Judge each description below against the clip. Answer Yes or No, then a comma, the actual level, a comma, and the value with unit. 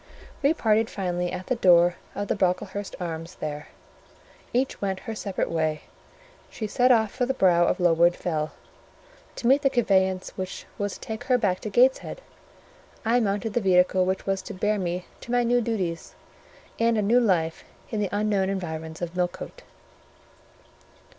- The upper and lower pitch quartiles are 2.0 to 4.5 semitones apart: Yes, average, 4.2 semitones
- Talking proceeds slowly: No, average, 165 wpm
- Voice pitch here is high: Yes, high, 195 Hz